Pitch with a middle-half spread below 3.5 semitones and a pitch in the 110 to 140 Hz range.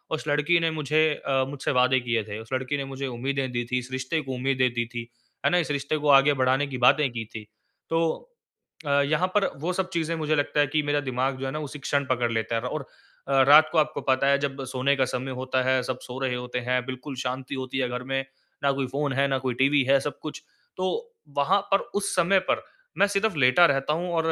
Yes: average, 2.7 semitones; low, 135 Hz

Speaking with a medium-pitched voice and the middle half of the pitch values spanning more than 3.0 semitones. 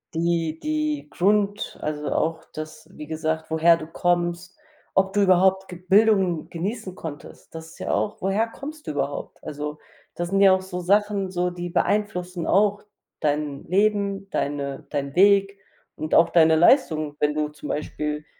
Yes: medium, 175 Hz; average, 4.2 semitones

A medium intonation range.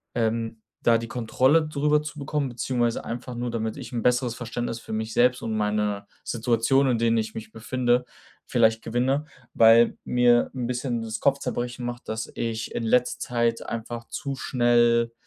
No: narrow, 1.6 semitones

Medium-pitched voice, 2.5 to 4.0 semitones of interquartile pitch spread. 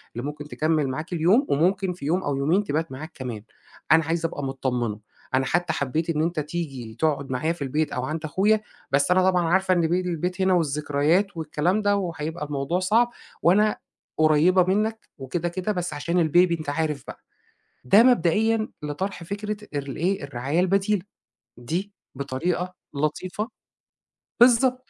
No: medium, 165 Hz; average, 4.4 semitones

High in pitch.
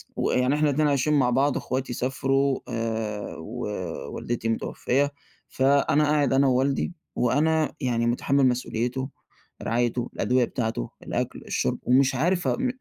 No: low, 130 Hz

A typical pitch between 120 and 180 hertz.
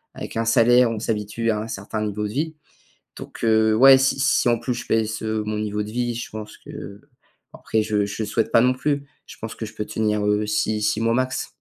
No: low, 110 Hz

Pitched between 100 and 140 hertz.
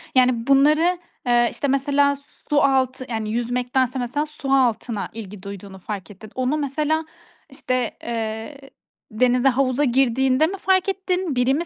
No: very high, 260 Hz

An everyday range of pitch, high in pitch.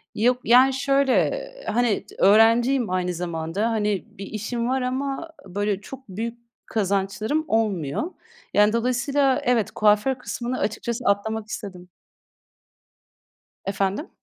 Yes: average, 4.0 semitones; high, 225 Hz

